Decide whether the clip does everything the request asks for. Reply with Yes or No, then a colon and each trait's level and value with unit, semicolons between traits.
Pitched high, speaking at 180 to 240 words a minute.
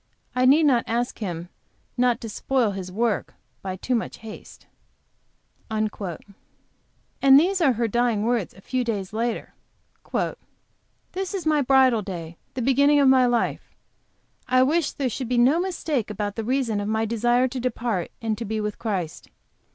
No: high, 240 Hz; average, 165 wpm